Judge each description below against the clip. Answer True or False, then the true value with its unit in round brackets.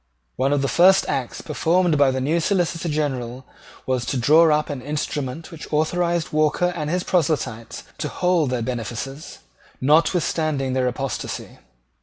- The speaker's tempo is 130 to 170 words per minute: True (150 wpm)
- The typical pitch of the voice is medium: True (150 Hz)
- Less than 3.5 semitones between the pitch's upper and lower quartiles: False (4.2 semitones)